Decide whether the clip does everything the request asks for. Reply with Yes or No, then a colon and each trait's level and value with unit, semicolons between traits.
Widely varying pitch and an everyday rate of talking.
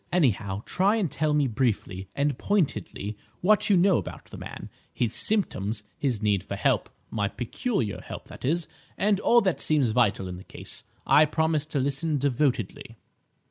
Yes: wide, 7.7 semitones; average, 170 wpm